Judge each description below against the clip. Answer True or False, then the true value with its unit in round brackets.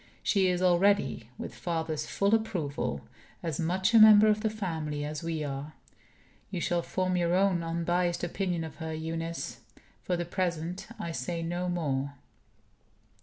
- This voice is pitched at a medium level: True (170 Hz)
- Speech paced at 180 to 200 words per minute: False (155 wpm)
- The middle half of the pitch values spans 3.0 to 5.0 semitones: False (2.5 semitones)